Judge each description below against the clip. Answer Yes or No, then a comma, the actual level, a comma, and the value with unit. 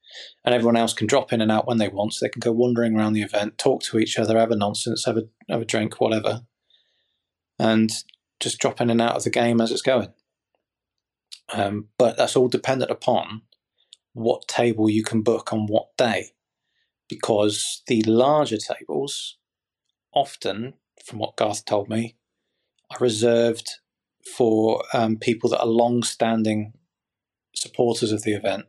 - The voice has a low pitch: Yes, low, 115 Hz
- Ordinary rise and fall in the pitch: No, narrow, 1.5 semitones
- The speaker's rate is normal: Yes, average, 165 wpm